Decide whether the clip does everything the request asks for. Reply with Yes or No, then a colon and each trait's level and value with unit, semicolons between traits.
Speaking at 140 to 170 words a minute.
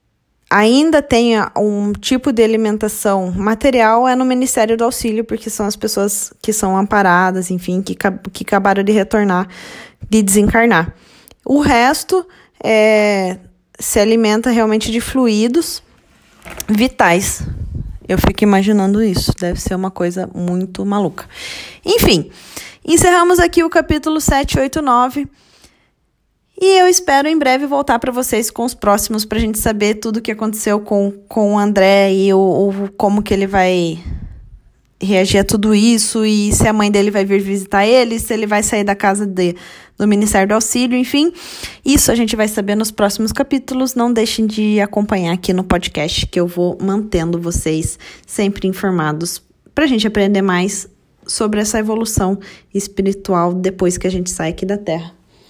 Yes: average, 160 wpm